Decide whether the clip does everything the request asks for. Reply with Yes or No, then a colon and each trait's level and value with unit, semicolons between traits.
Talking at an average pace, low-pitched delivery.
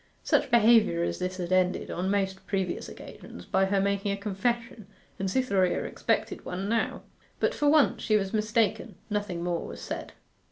No: average, 170 wpm; high, 200 Hz